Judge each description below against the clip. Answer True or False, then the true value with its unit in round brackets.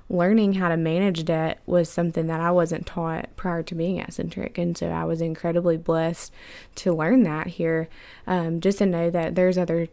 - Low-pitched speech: False (170 Hz)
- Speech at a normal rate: True (195 wpm)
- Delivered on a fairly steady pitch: True (1.7 semitones)